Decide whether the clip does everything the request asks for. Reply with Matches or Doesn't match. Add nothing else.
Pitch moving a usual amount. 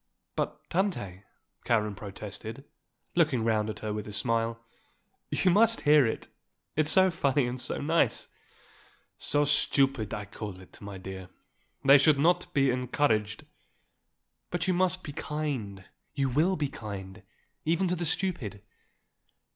Doesn't match